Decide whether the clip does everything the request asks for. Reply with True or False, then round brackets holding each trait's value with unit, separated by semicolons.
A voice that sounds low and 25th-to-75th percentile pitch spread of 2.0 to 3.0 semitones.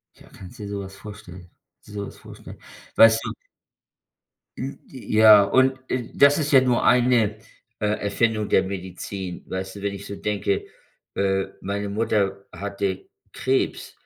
True (100 Hz; 2.7 semitones)